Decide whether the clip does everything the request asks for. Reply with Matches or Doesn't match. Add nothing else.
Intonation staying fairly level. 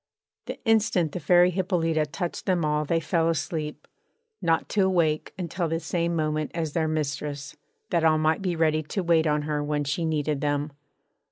Matches